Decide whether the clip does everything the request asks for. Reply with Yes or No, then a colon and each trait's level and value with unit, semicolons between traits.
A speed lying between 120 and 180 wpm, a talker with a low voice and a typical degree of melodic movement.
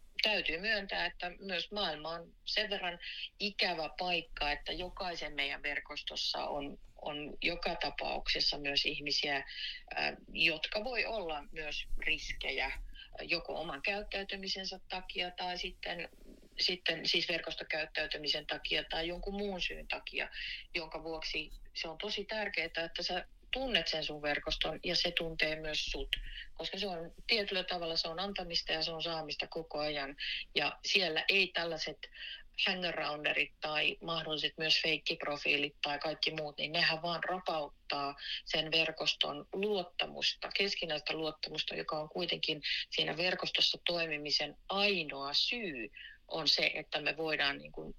No: average, 135 wpm; medium, 165 Hz; average, 3.0 semitones